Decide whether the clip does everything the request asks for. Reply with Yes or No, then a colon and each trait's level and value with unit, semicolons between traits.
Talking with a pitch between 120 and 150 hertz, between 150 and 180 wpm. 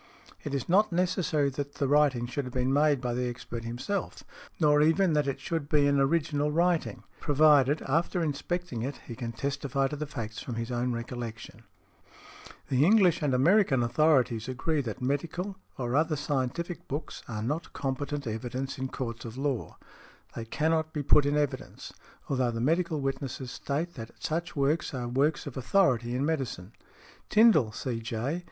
Yes: medium, 140 Hz; average, 170 wpm